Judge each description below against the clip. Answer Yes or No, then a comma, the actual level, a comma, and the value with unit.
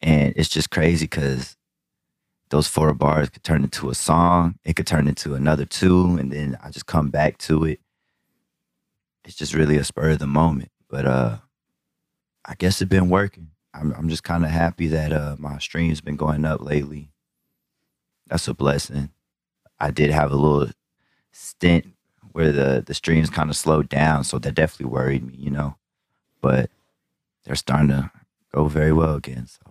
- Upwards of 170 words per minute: Yes, average, 180 wpm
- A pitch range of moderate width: No, narrow, 2.3 semitones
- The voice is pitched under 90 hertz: Yes, very low, 75 Hz